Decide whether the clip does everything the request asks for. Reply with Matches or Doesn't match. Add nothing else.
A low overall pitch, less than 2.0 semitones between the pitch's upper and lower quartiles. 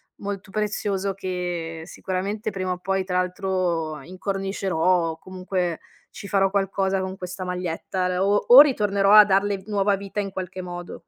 Doesn't match